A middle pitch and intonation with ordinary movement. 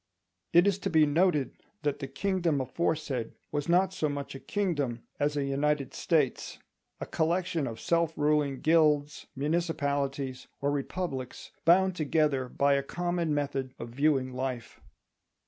Yes: medium, 145 Hz; average, 3.5 semitones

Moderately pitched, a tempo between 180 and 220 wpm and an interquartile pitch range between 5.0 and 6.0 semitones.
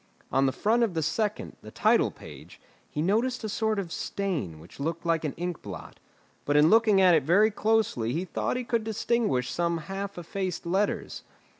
Yes: medium, 180 Hz; average, 190 wpm; wide, 5.5 semitones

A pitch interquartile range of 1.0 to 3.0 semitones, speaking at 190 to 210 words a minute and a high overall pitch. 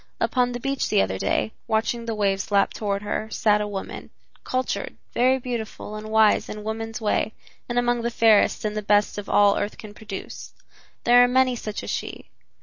Yes: average, 2.7 semitones; average, 195 wpm; high, 220 Hz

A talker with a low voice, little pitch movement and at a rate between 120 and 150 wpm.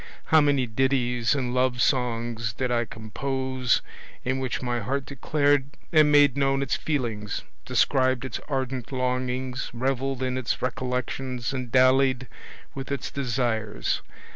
Yes: low, 130 Hz; narrow, 1.8 semitones; slow, 135 wpm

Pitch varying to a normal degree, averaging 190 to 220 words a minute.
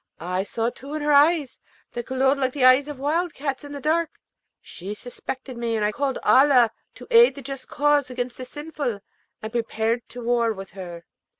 Yes: average, 3.6 semitones; average, 200 wpm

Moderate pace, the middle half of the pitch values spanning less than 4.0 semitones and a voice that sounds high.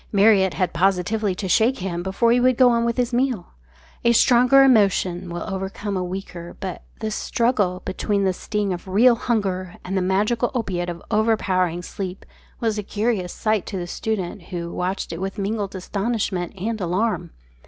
Yes: average, 175 wpm; average, 3.5 semitones; high, 195 Hz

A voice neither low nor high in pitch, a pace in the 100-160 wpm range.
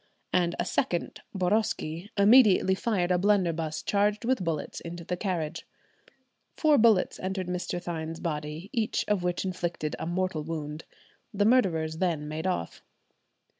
Yes: medium, 180 Hz; average, 140 wpm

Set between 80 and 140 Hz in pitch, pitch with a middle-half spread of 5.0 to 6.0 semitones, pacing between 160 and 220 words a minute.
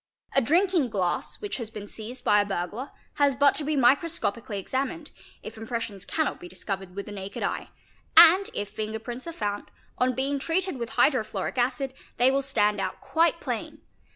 No: high, 245 Hz; wide, 5.4 semitones; average, 180 wpm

